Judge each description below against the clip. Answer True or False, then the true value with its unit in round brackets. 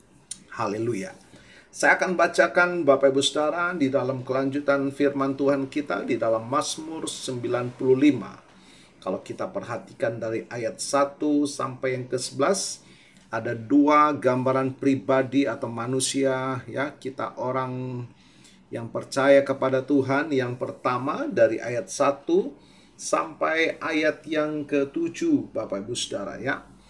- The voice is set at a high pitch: False (135 Hz)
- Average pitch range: False (2.3 semitones)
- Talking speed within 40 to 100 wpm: False (115 wpm)